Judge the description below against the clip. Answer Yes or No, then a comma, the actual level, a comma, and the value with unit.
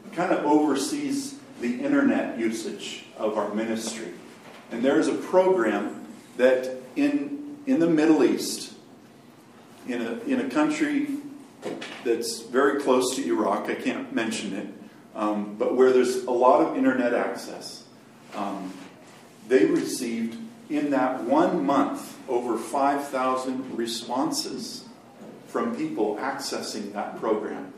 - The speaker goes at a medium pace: No, slow, 125 wpm